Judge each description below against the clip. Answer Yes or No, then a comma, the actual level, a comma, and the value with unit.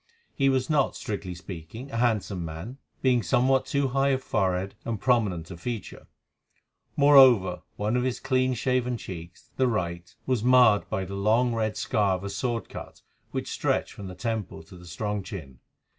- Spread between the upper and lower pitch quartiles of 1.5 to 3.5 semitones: No, wide, 5.4 semitones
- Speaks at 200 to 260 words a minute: No, average, 175 wpm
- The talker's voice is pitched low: Yes, low, 110 Hz